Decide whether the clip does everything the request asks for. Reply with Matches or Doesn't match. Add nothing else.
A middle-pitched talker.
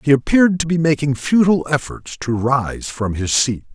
Matches